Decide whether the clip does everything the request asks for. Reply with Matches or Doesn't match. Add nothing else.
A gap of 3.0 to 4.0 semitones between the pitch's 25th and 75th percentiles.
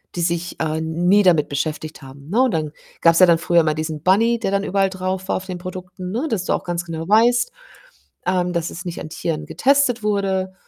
Matches